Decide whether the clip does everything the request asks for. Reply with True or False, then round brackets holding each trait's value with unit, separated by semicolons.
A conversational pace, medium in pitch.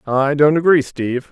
True (185 wpm; 145 Hz)